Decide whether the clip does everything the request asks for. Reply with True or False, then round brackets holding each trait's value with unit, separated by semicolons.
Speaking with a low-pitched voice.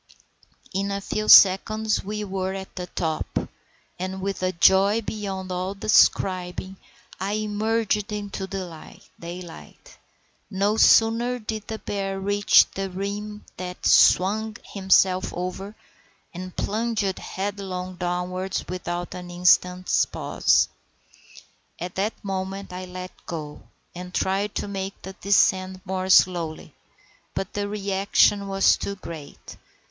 False (190 Hz)